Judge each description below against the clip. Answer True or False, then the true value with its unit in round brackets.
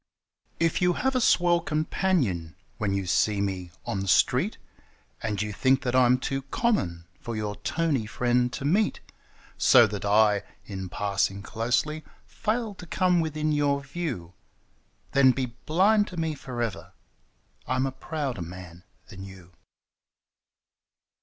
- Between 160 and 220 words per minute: False (145 wpm)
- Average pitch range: False (8.0 semitones)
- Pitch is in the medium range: False (125 Hz)